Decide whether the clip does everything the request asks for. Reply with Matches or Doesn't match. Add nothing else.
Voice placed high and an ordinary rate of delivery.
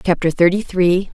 Doesn't match